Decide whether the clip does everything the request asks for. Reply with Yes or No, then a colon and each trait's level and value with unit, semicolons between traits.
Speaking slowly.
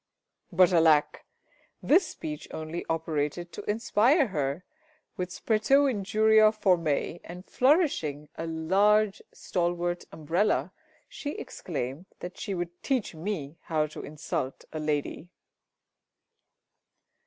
Yes: slow, 110 wpm